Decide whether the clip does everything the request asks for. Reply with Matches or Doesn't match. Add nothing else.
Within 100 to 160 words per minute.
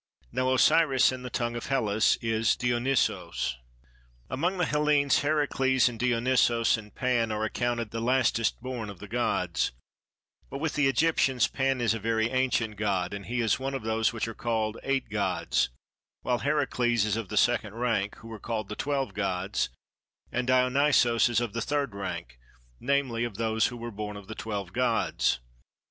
Doesn't match